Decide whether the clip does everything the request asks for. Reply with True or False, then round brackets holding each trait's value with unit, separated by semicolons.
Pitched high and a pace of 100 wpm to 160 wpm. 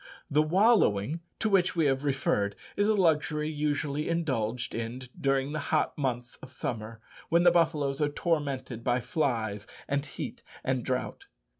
False (140 Hz; 155 wpm)